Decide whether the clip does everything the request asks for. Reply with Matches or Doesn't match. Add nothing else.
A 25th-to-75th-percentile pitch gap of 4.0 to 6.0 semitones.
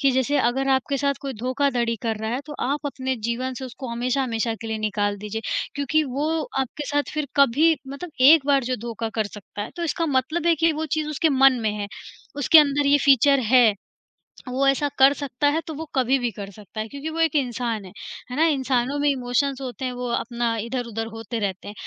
Doesn't match